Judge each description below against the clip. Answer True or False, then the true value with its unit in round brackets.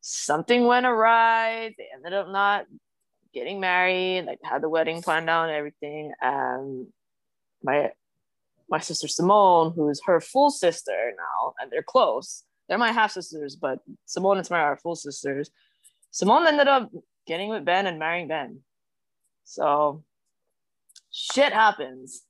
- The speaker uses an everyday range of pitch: False (6.4 semitones)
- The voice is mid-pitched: True (175 Hz)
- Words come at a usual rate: True (145 wpm)